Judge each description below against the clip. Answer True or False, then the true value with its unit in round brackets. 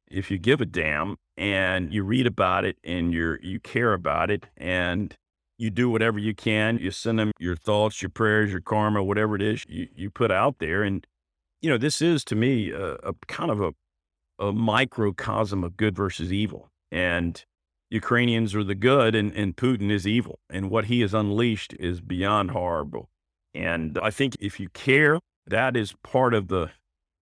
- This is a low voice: True (105 Hz)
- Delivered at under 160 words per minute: False (190 wpm)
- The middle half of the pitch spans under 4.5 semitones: True (3.9 semitones)